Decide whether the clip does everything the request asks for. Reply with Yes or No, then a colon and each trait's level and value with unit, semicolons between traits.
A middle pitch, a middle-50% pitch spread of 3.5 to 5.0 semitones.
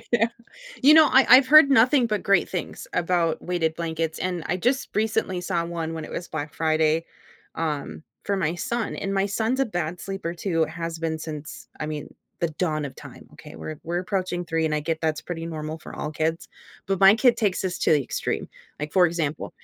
Yes: medium, 170 Hz; average, 3.8 semitones